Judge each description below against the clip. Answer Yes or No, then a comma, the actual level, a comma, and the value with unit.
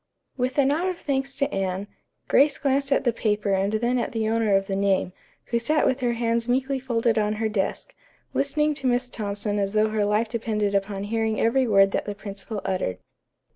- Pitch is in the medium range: No, high, 225 Hz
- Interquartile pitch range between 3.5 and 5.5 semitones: Yes, average, 4.1 semitones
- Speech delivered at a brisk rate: Yes, fast, 210 wpm